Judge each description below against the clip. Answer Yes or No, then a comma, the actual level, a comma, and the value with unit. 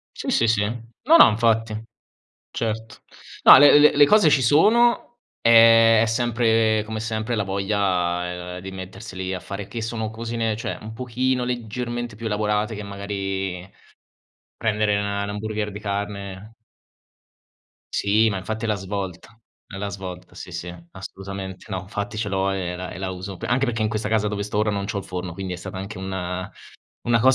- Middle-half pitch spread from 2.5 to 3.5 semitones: Yes, average, 2.8 semitones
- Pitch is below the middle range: Yes, low, 105 Hz